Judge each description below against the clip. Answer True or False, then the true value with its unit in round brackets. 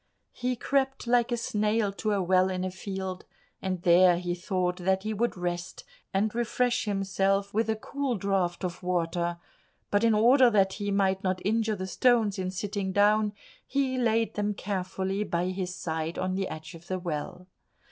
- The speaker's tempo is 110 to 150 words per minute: False (180 wpm)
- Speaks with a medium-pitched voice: False (195 Hz)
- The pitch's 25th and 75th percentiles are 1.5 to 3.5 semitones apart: True (2.9 semitones)